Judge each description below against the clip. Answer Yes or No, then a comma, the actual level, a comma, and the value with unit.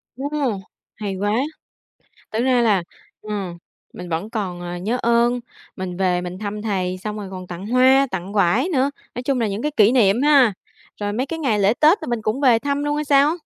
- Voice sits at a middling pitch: No, high, 215 Hz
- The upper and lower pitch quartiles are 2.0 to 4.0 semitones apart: No, average, 5.3 semitones